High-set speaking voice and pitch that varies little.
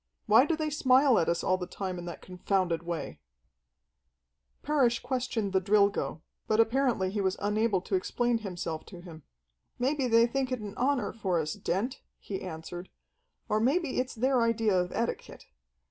No: high, 215 Hz; wide, 5.5 semitones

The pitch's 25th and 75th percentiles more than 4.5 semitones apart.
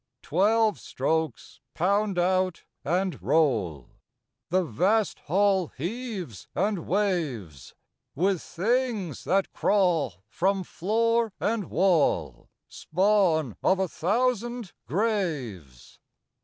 Yes: average, 5.0 semitones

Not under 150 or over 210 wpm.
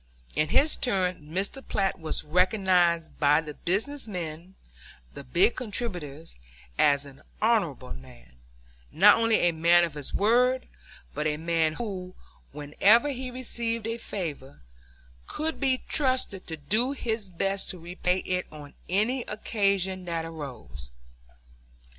No: slow, 135 wpm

